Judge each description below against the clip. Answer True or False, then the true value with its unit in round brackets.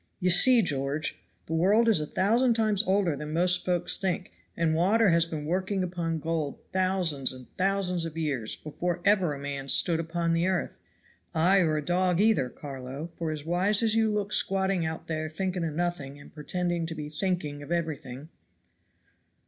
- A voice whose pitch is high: False (170 Hz)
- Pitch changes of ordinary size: True (3.5 semitones)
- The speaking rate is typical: True (180 wpm)